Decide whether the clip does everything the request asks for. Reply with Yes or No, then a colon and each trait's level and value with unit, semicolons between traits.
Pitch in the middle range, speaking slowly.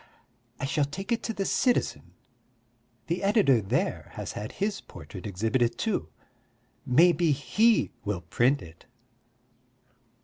Yes: medium, 145 Hz; slow, 125 wpm